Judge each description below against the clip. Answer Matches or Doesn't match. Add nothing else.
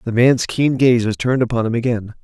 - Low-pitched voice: Matches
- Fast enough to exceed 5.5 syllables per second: Matches